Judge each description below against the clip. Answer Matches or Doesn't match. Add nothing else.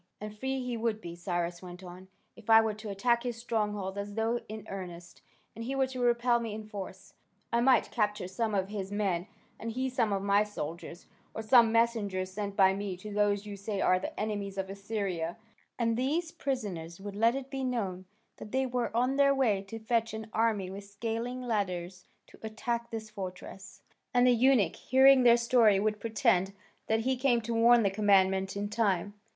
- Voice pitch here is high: Matches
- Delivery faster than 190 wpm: Matches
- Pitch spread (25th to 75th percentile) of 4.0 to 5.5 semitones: Doesn't match